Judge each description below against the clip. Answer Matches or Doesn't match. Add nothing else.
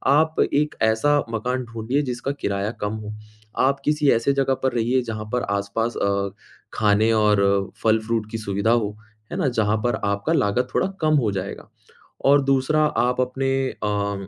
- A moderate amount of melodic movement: Matches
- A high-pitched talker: Doesn't match